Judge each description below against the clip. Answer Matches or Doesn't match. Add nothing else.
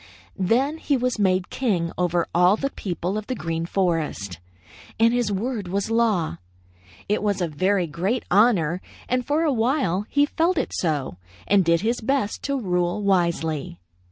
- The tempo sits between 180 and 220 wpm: Doesn't match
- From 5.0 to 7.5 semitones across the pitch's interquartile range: Matches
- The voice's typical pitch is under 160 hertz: Doesn't match